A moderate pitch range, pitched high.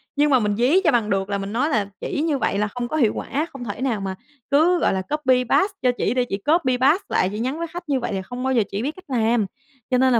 No: wide, 5.7 semitones; very high, 250 Hz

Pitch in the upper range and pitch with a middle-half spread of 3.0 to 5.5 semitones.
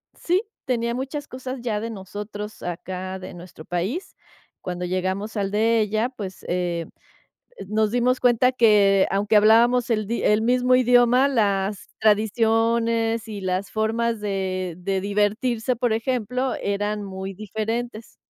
Yes: high, 215 Hz; average, 3.3 semitones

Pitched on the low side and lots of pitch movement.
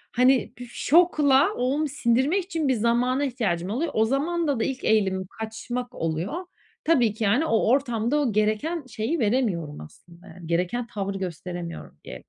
No: high, 240 Hz; wide, 6.0 semitones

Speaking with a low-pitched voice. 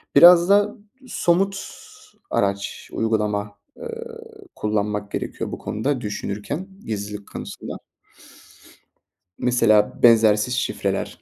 Yes: low, 115 Hz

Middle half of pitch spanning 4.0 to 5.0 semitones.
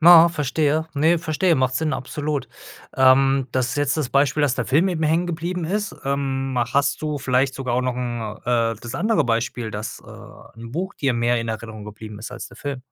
Yes: average, 4.4 semitones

